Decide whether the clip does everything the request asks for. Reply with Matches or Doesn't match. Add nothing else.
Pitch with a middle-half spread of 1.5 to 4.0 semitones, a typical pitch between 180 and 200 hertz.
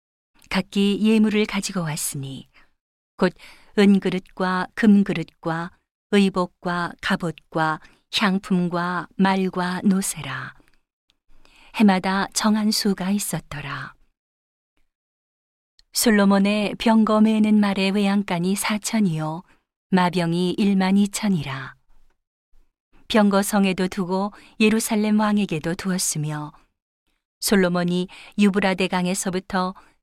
Matches